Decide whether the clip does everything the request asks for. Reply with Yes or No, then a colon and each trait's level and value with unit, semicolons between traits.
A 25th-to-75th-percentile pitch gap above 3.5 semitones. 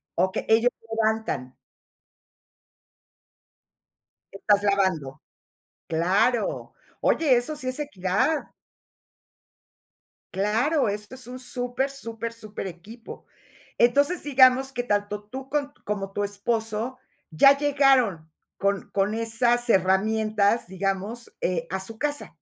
Yes: average, 4.4 semitones